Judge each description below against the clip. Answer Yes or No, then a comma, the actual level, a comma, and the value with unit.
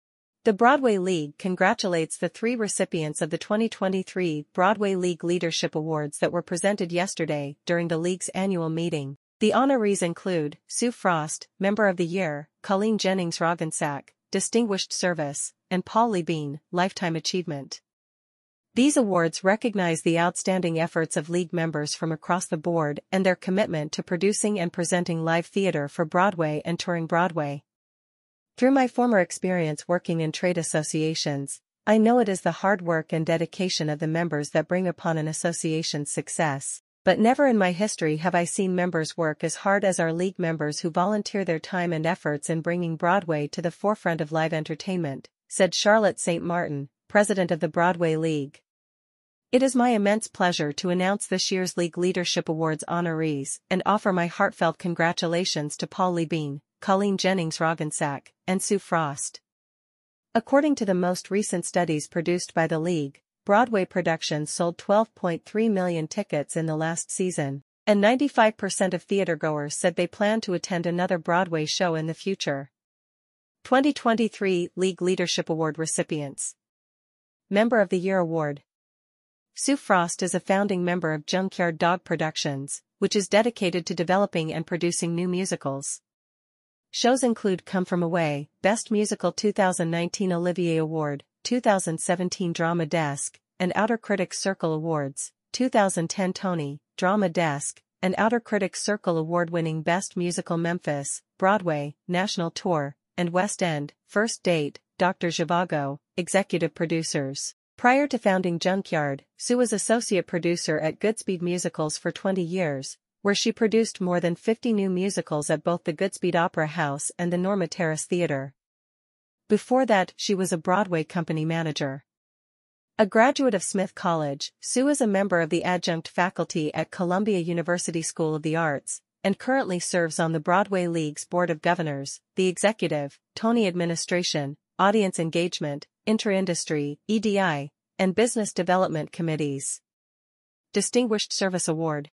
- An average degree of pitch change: Yes, average, 3.3 semitones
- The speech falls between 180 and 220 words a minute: No, average, 150 wpm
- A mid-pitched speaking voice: Yes, medium, 175 Hz